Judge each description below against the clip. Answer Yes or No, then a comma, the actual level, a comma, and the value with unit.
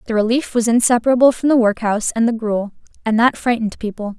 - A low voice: No, high, 230 Hz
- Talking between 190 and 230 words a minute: Yes, average, 200 wpm